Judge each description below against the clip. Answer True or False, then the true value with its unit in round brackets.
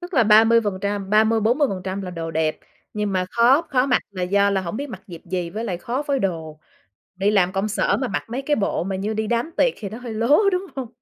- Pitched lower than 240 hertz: True (210 Hz)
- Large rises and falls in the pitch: False (4.5 semitones)